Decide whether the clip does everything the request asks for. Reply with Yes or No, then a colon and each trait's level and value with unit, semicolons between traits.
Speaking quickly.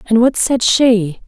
No: average, 190 wpm